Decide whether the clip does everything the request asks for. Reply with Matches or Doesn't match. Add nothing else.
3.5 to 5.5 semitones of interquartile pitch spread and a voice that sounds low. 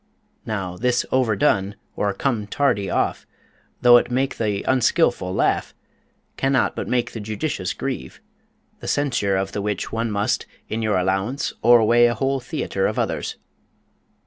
Matches